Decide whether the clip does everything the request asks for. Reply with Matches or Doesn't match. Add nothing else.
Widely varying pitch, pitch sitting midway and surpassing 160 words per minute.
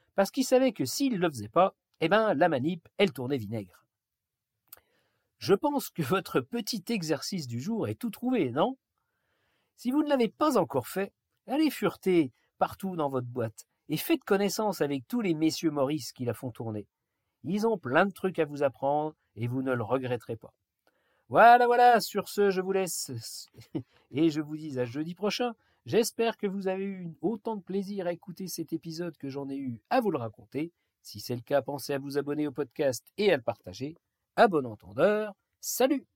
Matches